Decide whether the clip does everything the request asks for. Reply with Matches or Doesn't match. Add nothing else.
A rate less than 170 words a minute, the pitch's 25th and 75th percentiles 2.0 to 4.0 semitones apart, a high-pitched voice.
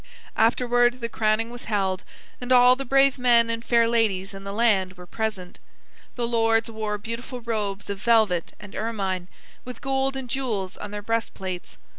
Doesn't match